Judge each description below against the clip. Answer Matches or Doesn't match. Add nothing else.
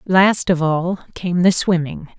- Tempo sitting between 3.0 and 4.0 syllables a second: Matches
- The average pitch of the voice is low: Doesn't match